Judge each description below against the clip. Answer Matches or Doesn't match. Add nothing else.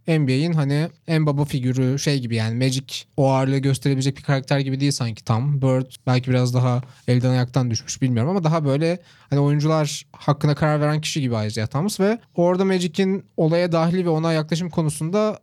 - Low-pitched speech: Doesn't match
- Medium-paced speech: Doesn't match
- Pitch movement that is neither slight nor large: Matches